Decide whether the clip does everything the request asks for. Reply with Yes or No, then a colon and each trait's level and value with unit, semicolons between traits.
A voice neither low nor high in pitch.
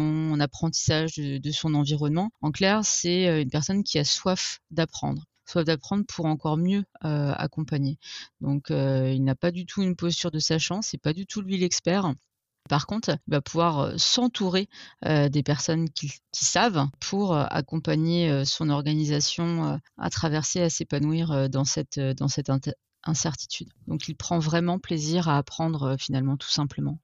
Yes: medium, 155 Hz